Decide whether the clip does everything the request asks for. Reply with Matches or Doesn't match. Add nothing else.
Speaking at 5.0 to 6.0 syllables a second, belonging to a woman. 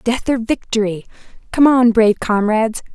Matches